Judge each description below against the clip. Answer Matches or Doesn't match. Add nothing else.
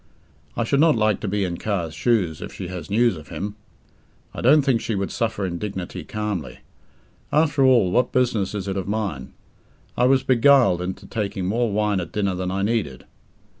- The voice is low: Matches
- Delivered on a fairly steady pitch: Doesn't match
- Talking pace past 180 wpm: Matches